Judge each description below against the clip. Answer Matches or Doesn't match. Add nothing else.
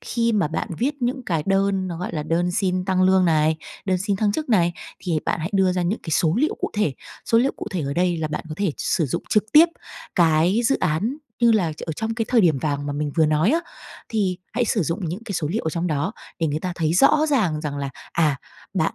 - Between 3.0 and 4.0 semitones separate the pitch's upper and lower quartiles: Doesn't match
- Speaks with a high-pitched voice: Doesn't match